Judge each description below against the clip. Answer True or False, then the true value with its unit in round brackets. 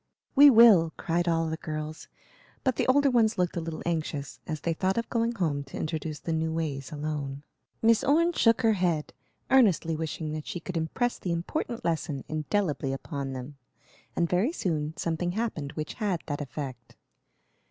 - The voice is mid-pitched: True (165 Hz)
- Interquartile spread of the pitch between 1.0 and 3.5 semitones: False (5.3 semitones)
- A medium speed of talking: True (175 wpm)